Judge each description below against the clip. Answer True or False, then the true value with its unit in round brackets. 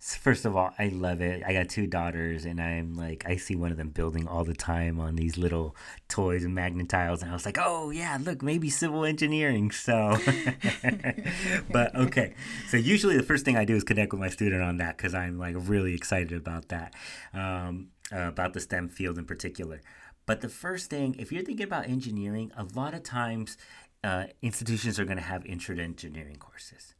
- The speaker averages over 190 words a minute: True (205 wpm)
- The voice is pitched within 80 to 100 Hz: True (95 Hz)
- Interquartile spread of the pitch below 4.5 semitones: False (5.2 semitones)